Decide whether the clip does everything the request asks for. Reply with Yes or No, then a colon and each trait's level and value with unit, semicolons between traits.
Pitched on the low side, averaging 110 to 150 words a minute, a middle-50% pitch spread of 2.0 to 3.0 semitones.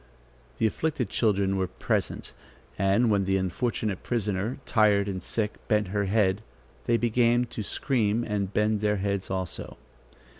Yes: low, 105 Hz; average, 145 wpm; narrow, 2.6 semitones